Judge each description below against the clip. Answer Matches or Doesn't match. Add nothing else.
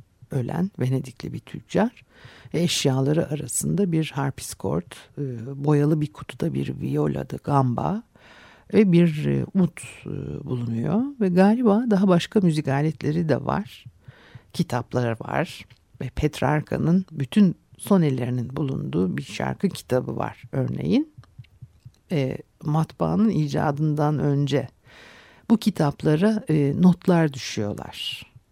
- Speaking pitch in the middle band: Matches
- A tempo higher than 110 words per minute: Doesn't match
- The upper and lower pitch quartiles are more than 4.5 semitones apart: Matches